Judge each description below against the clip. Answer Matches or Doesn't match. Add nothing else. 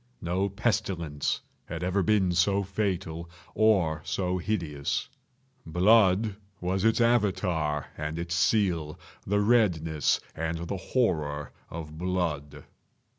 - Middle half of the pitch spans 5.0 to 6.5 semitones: Doesn't match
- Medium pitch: Doesn't match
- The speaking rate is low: Matches